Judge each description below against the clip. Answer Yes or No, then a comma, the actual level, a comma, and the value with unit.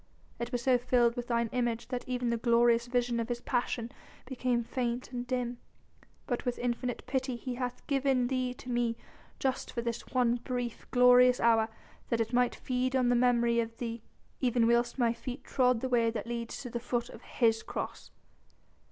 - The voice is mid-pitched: No, high, 245 Hz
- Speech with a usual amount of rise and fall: No, narrow, 1.2 semitones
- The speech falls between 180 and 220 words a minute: Yes, average, 190 wpm